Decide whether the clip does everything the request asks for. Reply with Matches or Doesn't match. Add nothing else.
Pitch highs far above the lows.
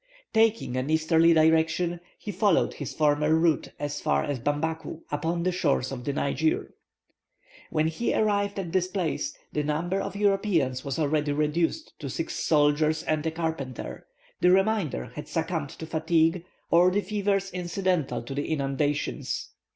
Doesn't match